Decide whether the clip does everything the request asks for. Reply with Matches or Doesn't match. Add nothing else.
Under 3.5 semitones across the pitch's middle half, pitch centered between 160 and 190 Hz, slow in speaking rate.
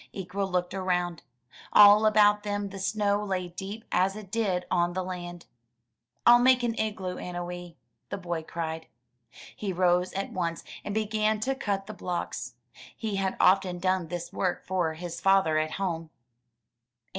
Doesn't match